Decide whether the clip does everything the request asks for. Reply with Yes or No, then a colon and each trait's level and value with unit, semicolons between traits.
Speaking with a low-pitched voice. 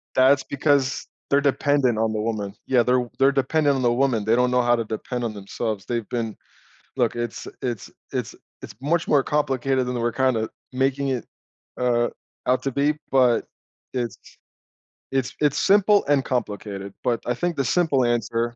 Yes: low, 125 Hz